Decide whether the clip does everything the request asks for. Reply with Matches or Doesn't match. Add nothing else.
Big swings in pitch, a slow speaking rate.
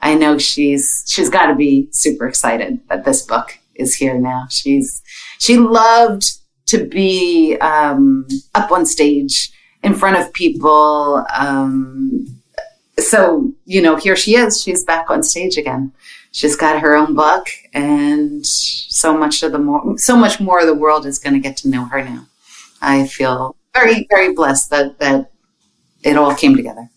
Doesn't match